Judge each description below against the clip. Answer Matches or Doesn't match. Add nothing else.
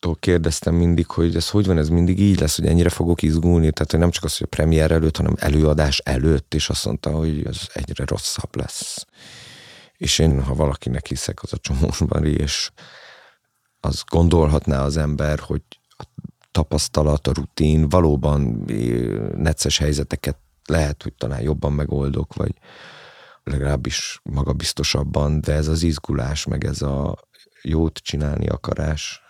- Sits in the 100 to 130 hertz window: Doesn't match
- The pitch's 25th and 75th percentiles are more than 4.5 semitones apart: Doesn't match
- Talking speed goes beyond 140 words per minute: Matches